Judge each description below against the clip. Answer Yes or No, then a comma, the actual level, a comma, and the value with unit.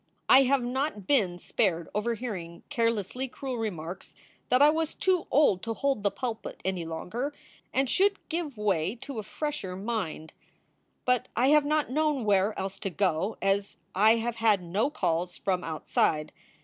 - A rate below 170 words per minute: Yes, average, 160 wpm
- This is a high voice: Yes, high, 220 Hz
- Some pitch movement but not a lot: No, wide, 6.2 semitones